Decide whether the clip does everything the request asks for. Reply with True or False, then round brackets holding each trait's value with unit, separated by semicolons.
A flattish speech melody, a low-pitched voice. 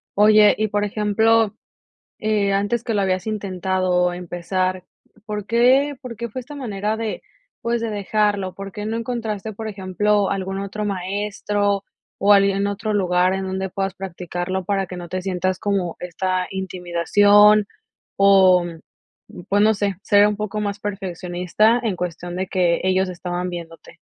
False (2.2 semitones; 195 Hz)